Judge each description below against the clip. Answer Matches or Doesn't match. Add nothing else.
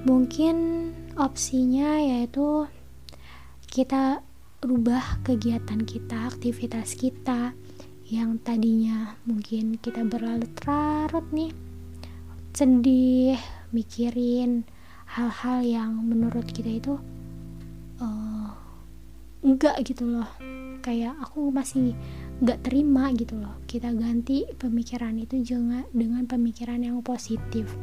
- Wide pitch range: Doesn't match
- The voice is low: Doesn't match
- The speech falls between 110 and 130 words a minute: Doesn't match